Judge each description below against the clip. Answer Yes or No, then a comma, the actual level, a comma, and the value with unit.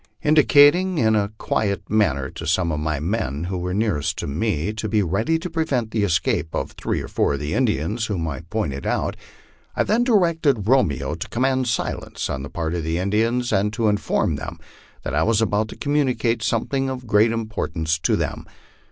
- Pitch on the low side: Yes, low, 105 Hz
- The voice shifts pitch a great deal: Yes, wide, 7.0 semitones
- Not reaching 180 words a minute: No, fast, 205 wpm